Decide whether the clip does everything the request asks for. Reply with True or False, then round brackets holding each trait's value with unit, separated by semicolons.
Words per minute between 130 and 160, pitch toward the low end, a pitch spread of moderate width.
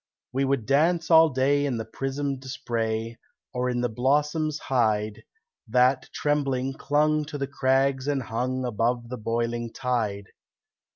True (140 wpm; 130 Hz; 3.3 semitones)